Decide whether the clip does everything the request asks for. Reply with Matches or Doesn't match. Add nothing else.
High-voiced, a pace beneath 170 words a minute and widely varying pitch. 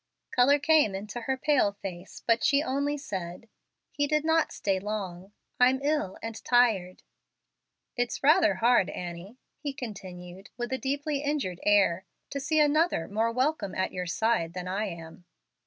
Matches